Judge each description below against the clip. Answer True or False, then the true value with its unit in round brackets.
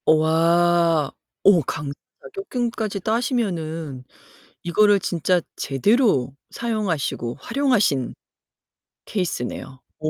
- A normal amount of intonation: False (5.9 semitones)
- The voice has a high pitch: False (175 Hz)